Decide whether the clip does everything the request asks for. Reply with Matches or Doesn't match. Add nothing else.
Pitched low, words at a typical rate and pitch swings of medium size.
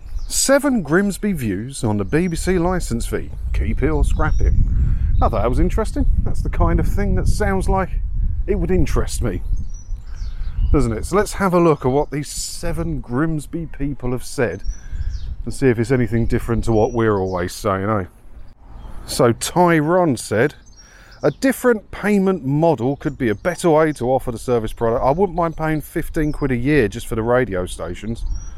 Doesn't match